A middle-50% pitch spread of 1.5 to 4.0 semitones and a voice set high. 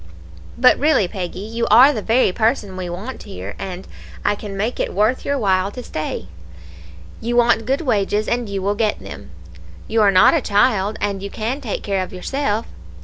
Yes: average, 3.6 semitones; high, 210 Hz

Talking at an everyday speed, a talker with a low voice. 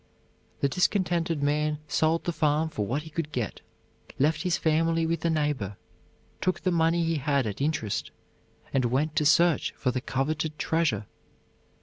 No: average, 160 wpm; medium, 155 Hz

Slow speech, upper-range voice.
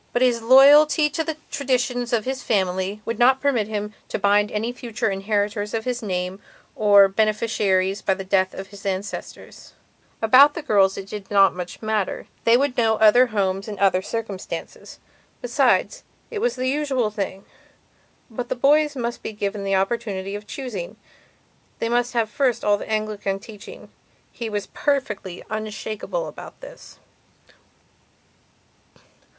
No: average, 155 wpm; high, 215 Hz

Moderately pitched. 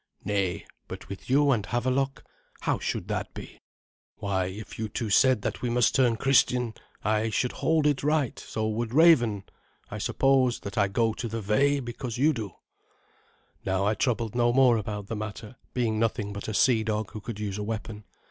No: low, 115 Hz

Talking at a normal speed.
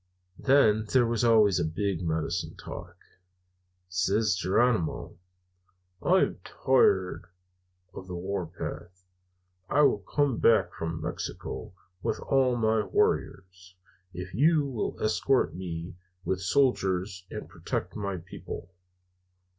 No: slow, 115 wpm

